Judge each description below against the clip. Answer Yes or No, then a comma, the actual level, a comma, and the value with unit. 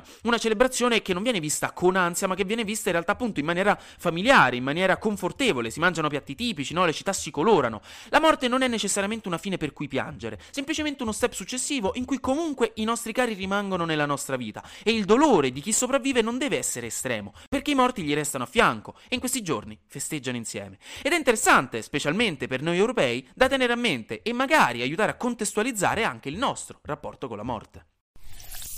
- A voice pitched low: No, high, 200 Hz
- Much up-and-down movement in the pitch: Yes, wide, 8.8 semitones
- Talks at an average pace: No, fast, 210 wpm